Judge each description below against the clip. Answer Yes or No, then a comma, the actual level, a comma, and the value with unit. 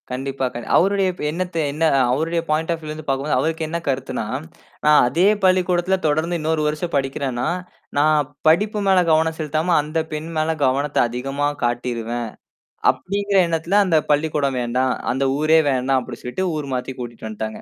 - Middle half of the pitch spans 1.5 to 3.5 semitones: No, average, 3.9 semitones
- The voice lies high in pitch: No, medium, 155 Hz